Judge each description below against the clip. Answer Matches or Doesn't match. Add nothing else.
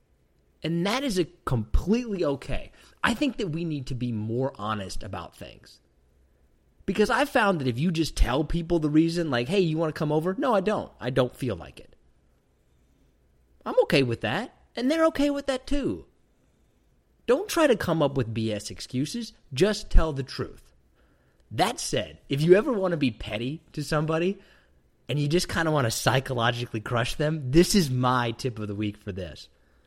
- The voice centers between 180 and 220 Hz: Doesn't match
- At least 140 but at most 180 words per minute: Doesn't match